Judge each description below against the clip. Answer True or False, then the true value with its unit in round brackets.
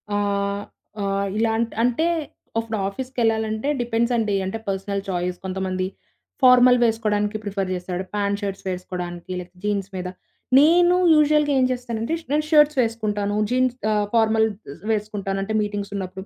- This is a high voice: True (210 Hz)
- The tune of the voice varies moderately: True (3.2 semitones)